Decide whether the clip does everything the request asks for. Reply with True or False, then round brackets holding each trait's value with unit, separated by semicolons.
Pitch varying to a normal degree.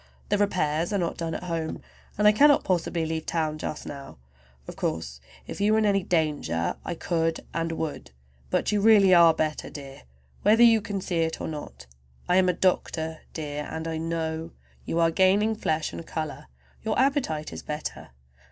True (3.9 semitones)